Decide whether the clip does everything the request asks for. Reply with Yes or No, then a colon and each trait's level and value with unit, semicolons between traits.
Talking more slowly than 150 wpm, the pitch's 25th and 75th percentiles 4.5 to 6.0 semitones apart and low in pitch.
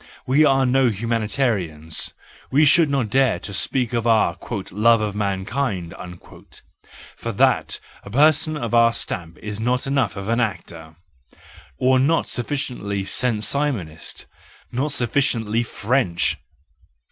Yes: slow, 135 wpm; average, 4.9 semitones; low, 115 Hz